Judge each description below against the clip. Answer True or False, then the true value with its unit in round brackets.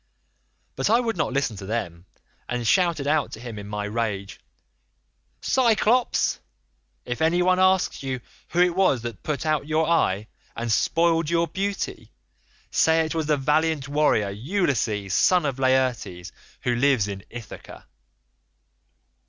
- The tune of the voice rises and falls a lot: True (6.7 semitones)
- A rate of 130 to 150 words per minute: True (145 wpm)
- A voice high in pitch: False (140 Hz)